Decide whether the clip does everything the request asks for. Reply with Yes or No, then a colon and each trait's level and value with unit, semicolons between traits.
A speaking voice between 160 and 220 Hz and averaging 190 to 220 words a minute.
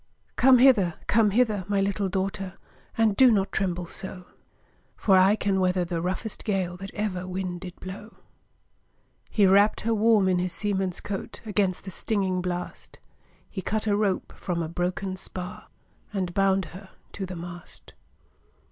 No: high, 190 Hz; average, 160 wpm